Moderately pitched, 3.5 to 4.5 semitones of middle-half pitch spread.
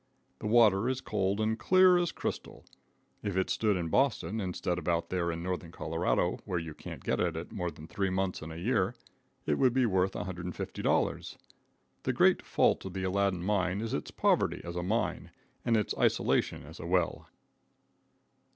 No: very low, 95 Hz; average, 3.8 semitones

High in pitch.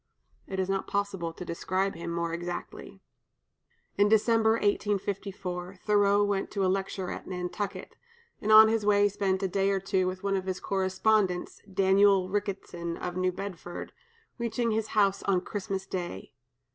Yes: high, 195 Hz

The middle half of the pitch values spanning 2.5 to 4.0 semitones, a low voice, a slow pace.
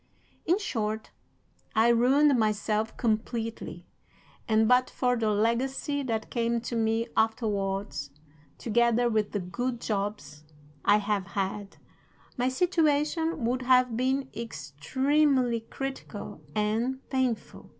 No: average, 3.4 semitones; high, 230 Hz; slow, 110 wpm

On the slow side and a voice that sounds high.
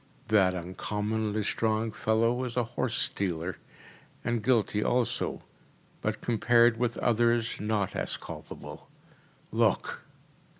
No: slow, 110 wpm; low, 110 Hz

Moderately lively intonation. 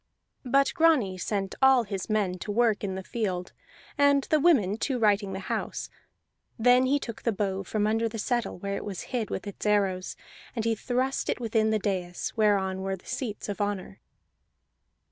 Yes: average, 3.8 semitones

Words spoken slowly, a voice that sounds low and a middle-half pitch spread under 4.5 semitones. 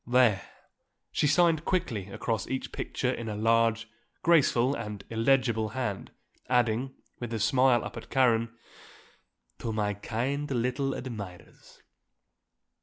Yes: slow, 120 wpm; low, 120 Hz; average, 3.1 semitones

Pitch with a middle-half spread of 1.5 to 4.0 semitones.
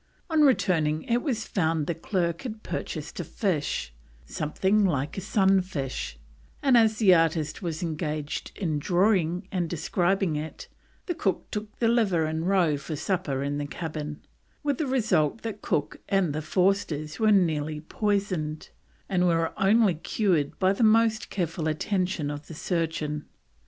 No: average, 4.8 semitones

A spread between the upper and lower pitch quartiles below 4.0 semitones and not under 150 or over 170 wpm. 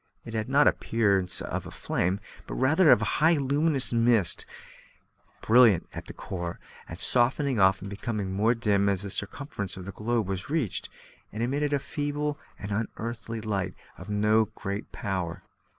No: average, 4.9 semitones; average, 165 wpm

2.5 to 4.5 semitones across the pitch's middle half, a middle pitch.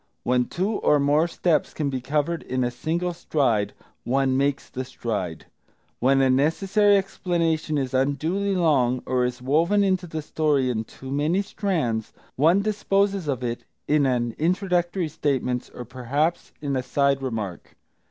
No: average, 5.2 semitones; medium, 145 Hz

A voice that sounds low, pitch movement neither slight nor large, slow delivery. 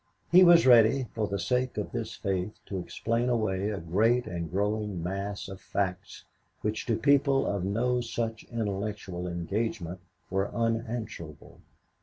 No: low, 105 Hz; average, 3.5 semitones; average, 145 wpm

